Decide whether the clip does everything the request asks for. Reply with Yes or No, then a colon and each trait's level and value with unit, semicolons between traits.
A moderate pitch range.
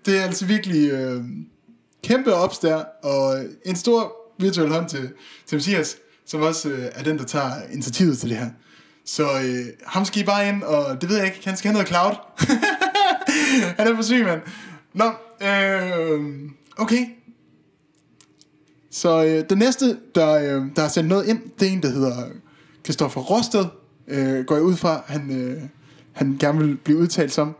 No: wide, 5.8 semitones